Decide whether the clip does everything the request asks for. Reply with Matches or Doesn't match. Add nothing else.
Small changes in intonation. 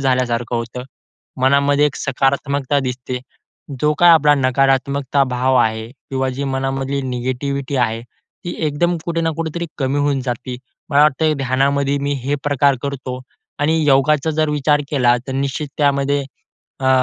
Matches